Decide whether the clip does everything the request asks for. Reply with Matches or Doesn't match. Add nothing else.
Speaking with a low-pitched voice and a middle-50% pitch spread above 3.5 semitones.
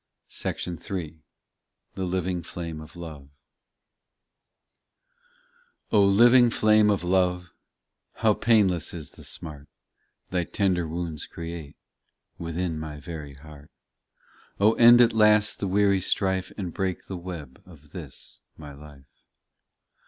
Matches